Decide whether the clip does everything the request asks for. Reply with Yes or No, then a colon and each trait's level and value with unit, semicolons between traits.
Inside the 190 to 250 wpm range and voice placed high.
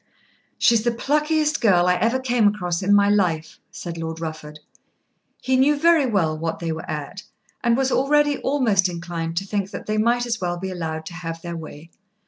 Yes: average, 200 wpm; high, 195 Hz